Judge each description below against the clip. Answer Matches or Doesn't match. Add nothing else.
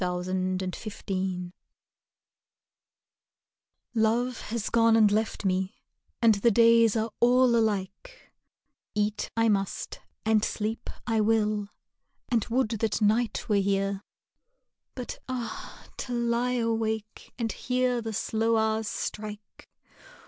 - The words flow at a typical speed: Doesn't match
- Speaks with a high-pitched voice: Matches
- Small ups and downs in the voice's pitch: Matches